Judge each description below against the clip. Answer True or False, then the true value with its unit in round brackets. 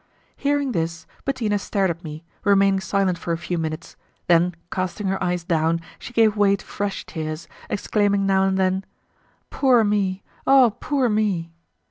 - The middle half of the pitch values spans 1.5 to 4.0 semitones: True (3.5 semitones)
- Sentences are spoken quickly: False (160 wpm)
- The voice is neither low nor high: False (195 Hz)